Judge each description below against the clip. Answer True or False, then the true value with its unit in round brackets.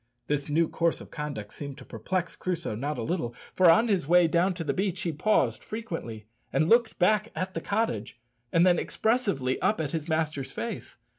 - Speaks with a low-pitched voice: False (170 Hz)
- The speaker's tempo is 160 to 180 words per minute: False (200 wpm)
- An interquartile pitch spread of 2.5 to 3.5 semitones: False (4.7 semitones)